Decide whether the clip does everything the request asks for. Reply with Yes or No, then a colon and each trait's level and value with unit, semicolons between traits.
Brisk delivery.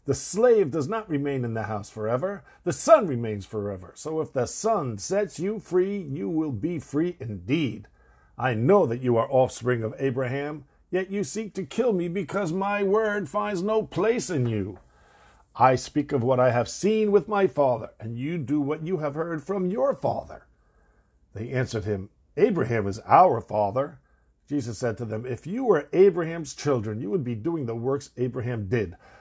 No: average, 185 wpm